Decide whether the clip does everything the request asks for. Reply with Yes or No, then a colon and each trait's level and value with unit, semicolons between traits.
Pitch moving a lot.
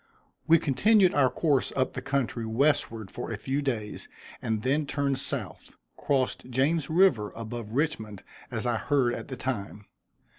No: average, 4.2 semitones